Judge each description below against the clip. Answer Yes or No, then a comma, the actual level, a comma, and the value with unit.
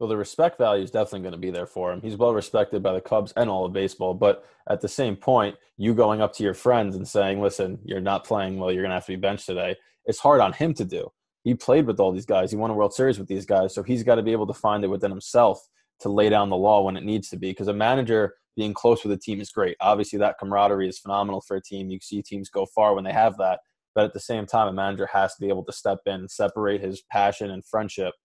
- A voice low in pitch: Yes, low, 100 Hz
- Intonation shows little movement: Yes, narrow, 2.2 semitones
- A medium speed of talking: No, fast, 290 wpm